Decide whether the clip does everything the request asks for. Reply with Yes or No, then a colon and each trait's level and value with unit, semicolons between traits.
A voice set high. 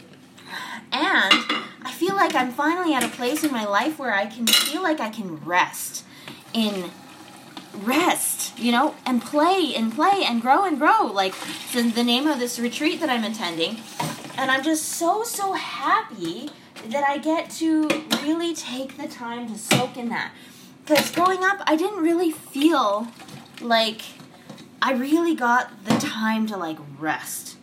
Yes: very high, 260 Hz